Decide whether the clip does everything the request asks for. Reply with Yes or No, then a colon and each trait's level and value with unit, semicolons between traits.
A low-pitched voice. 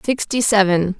No: high, 205 Hz